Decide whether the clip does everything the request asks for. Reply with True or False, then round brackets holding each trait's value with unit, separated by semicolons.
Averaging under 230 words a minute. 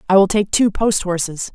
False (235 wpm)